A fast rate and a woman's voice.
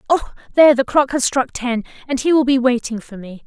Yes: fast, 245 wpm; female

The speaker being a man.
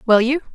No: female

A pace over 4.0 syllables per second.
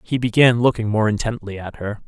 Yes: 5.6 syllables/s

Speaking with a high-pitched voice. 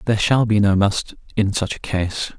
No: low, 100 Hz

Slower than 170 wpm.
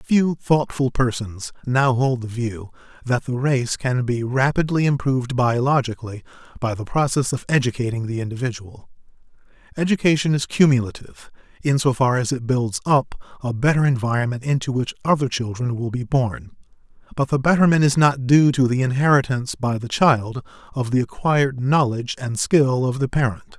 Yes: average, 160 wpm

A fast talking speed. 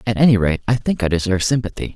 Yes: fast, 245 wpm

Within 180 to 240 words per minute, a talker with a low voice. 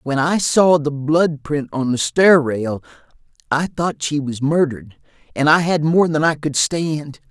No: average, 190 wpm; medium, 150 Hz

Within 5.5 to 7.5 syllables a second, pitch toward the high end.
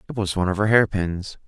No: 6.6 syllables/s; low, 100 Hz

